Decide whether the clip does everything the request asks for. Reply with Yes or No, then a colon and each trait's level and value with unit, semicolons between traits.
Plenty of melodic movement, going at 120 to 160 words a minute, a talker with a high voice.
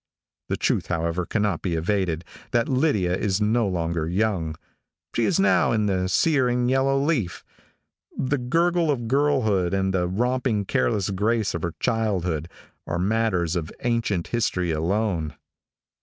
No: wide, 5.7 semitones; average, 145 wpm; low, 105 Hz